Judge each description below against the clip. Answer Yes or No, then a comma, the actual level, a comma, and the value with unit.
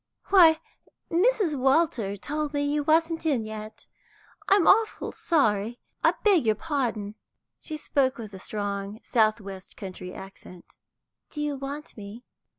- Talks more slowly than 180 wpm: Yes, average, 140 wpm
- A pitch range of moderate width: No, wide, 7.1 semitones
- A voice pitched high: Yes, very high, 265 Hz